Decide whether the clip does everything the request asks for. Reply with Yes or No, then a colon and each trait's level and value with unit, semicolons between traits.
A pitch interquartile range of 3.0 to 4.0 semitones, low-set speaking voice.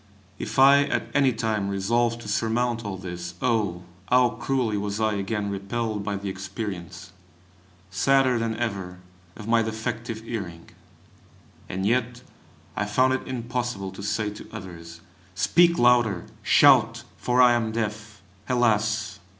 Yes: average, 3.4 semitones; low, 110 Hz